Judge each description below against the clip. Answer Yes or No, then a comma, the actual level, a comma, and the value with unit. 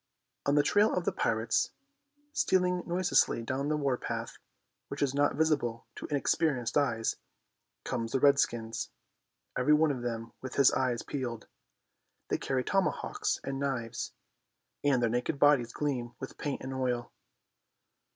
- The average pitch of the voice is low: Yes, low, 130 Hz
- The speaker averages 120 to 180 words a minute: Yes, average, 145 wpm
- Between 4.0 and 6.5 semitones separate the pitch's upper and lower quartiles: No, average, 3.4 semitones